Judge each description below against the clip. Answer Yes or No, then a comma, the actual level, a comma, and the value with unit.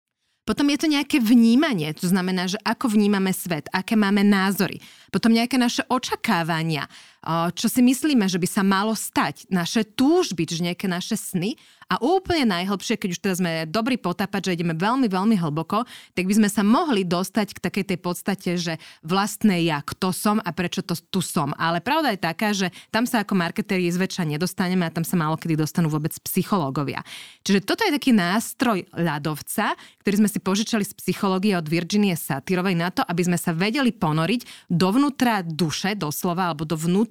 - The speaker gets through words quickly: Yes, fast, 180 wpm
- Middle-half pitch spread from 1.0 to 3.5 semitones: No, average, 4.1 semitones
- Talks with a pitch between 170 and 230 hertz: Yes, high, 190 Hz